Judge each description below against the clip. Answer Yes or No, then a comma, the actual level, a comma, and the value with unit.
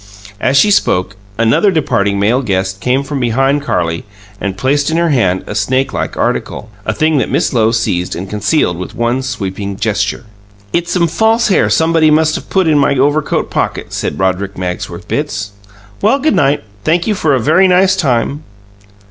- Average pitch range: No, wide, 7.8 semitones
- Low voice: Yes, low, 130 Hz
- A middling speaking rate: Yes, average, 180 wpm